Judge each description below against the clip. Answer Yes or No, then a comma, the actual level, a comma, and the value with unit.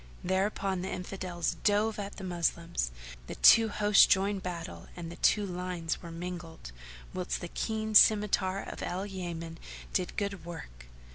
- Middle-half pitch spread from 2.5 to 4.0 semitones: Yes, average, 2.8 semitones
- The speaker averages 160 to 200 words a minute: No, average, 150 wpm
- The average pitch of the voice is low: No, medium, 185 Hz